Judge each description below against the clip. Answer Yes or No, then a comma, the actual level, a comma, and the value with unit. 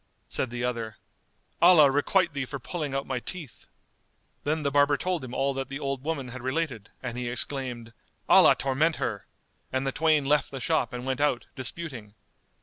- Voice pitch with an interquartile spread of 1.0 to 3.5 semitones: Yes, average, 3.2 semitones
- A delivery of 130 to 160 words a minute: No, average, 185 wpm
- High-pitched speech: No, low, 135 Hz